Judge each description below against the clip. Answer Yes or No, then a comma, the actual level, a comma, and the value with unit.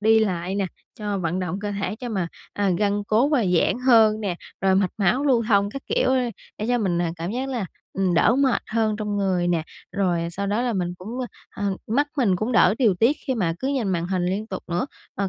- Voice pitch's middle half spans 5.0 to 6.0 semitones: No, average, 3.8 semitones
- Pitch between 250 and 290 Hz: No, high, 205 Hz